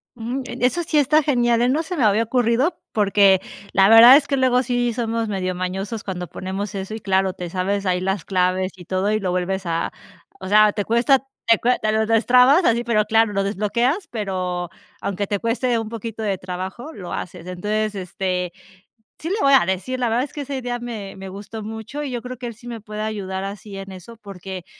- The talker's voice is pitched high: Yes, high, 215 Hz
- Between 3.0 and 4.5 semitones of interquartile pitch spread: Yes, average, 4.1 semitones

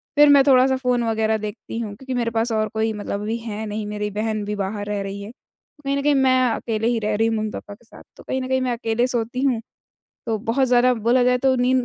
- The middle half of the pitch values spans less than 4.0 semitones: Yes, average, 2.9 semitones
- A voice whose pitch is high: Yes, high, 225 Hz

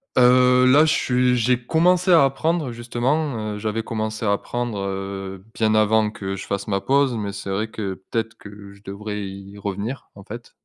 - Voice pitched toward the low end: Yes, low, 110 Hz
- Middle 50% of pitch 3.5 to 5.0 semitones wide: Yes, average, 4.0 semitones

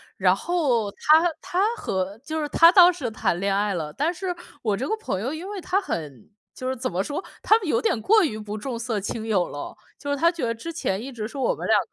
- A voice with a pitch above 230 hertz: Yes, very high, 255 Hz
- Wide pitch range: Yes, wide, 8.4 semitones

